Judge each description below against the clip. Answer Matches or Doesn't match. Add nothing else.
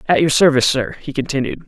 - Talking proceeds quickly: Matches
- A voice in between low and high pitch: Matches